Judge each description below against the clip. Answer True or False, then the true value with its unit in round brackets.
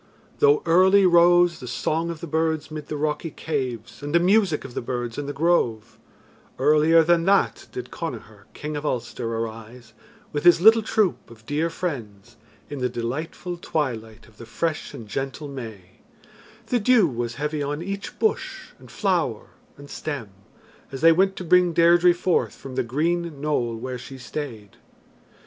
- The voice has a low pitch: False (150 Hz)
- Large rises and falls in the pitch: True (5.9 semitones)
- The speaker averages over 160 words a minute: True (170 wpm)